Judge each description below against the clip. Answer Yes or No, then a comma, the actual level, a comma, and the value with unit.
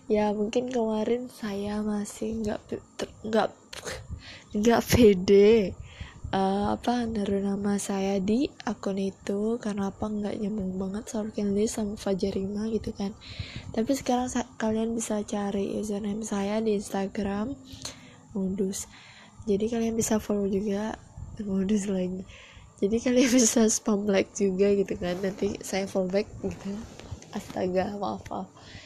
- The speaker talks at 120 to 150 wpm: Yes, average, 135 wpm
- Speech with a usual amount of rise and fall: No, narrow, 2.0 semitones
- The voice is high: Yes, high, 210 Hz